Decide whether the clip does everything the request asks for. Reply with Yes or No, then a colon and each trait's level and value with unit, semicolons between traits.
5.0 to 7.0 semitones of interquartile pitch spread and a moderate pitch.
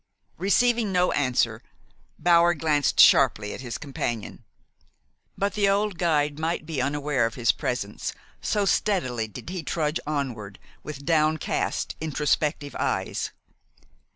Yes: average, 5.3 semitones; medium, 150 Hz